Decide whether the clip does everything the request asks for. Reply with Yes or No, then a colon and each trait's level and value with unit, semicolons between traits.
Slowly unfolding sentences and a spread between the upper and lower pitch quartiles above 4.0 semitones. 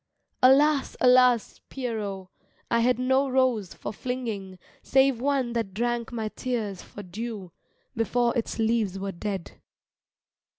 No: slow, 125 wpm; average, 3.6 semitones